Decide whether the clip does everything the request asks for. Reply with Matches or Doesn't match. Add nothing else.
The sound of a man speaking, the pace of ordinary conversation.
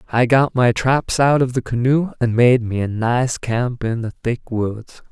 Doesn't match